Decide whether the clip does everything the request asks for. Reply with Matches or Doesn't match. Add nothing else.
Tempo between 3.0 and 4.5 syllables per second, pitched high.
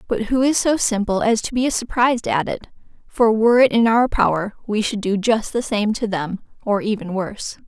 Doesn't match